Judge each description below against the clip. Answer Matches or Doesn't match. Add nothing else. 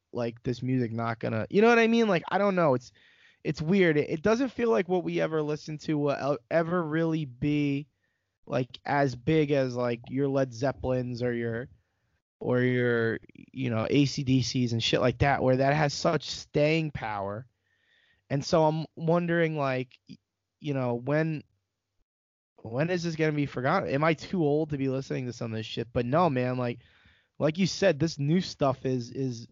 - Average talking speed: Matches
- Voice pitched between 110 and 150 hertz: Matches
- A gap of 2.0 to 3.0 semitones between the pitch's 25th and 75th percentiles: Doesn't match